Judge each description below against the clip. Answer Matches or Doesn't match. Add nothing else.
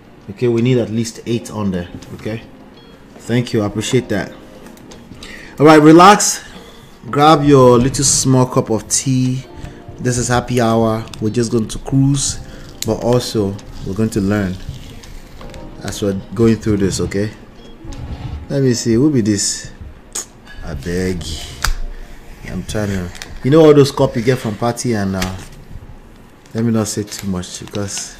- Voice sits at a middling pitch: Doesn't match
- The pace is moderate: Matches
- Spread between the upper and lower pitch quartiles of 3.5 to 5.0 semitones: Matches